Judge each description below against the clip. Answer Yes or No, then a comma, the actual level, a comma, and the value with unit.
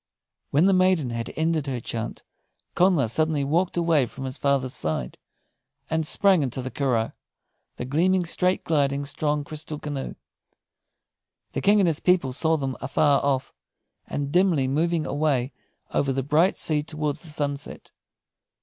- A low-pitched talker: No, medium, 150 Hz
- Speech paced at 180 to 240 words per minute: No, average, 150 wpm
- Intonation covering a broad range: No, average, 3.4 semitones